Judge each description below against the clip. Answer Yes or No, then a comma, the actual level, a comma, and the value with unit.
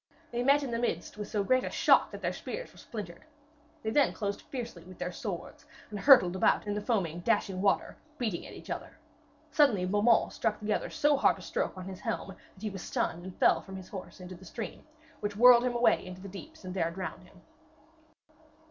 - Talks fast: Yes, fast, 220 wpm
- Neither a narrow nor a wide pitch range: Yes, average, 4.4 semitones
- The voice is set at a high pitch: Yes, high, 205 Hz